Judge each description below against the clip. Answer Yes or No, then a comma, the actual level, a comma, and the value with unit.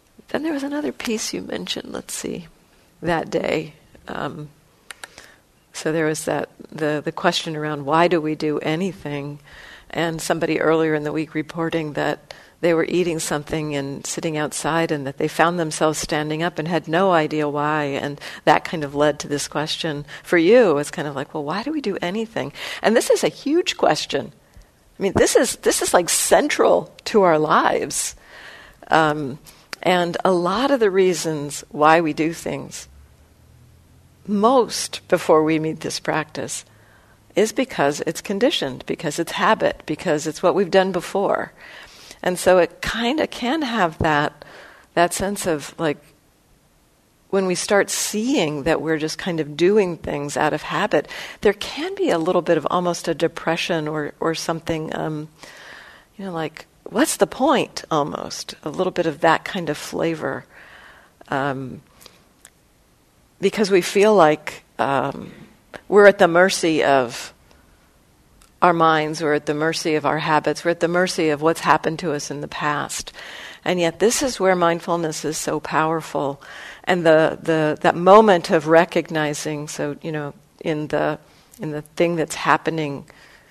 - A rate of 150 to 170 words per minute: Yes, average, 165 wpm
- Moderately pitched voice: Yes, medium, 160 Hz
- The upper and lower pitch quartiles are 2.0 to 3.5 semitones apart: Yes, average, 3.1 semitones